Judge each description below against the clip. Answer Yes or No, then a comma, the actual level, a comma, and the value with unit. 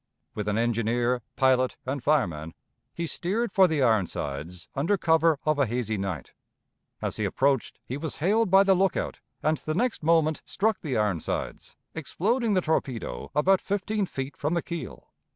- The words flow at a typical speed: Yes, average, 165 wpm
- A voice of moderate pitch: Yes, medium, 150 Hz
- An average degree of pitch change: No, wide, 7.5 semitones